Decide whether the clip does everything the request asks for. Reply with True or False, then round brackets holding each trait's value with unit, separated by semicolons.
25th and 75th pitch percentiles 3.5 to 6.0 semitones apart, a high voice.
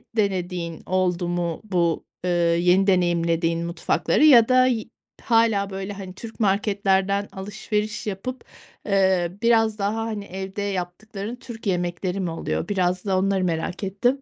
False (3.0 semitones; 195 Hz)